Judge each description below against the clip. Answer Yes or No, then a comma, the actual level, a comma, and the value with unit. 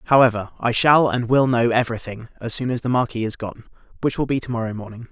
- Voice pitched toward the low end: Yes, low, 120 Hz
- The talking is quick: Yes, fast, 245 wpm